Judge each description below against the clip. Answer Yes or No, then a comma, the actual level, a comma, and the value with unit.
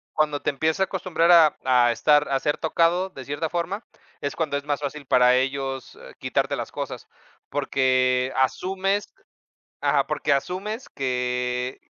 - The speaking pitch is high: No, medium, 145 Hz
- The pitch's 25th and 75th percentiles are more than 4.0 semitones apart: Yes, average, 4.5 semitones